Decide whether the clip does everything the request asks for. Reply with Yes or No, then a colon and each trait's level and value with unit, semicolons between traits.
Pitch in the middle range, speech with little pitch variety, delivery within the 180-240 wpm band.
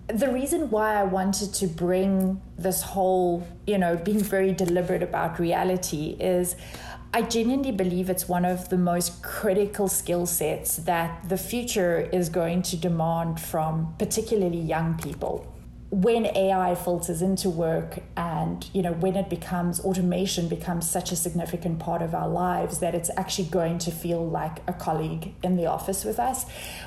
No: medium, 180 Hz; narrow, 2.1 semitones; average, 165 wpm